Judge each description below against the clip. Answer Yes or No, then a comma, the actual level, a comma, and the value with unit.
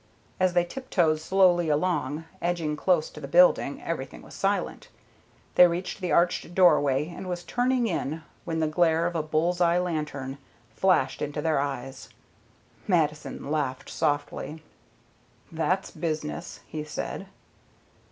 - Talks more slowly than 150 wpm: Yes, slow, 135 wpm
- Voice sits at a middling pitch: Yes, medium, 165 Hz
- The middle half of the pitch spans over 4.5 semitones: No, average, 2.9 semitones